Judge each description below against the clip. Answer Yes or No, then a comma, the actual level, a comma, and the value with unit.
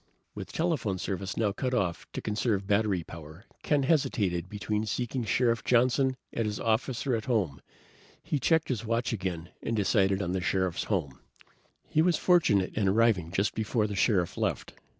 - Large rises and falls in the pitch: No, average, 4.5 semitones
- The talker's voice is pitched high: No, low, 105 Hz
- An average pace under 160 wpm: No, average, 170 wpm